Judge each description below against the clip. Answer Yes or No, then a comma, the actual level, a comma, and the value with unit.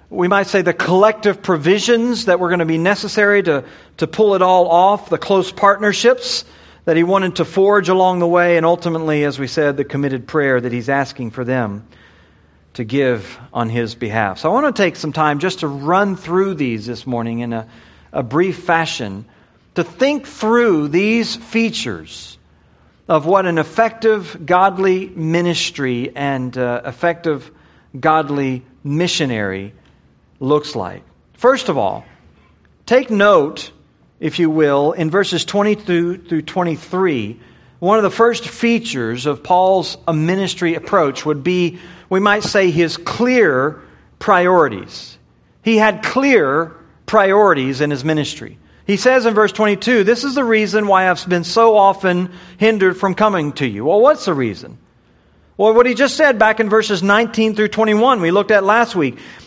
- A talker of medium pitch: Yes, medium, 175 Hz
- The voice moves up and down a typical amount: No, wide, 6.7 semitones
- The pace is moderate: Yes, average, 165 wpm